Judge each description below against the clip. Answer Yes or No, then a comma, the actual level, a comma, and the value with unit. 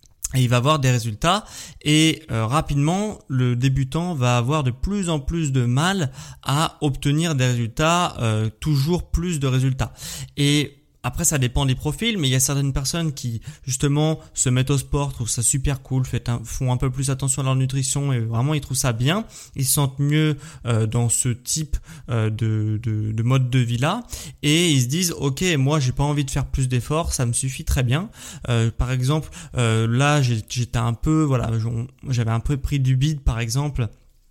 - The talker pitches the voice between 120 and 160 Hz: Yes, low, 135 Hz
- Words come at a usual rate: Yes, average, 190 wpm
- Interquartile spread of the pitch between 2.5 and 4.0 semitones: Yes, average, 3.4 semitones